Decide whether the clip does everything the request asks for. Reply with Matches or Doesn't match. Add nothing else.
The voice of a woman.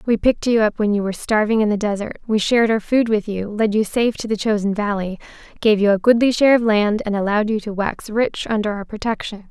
Matches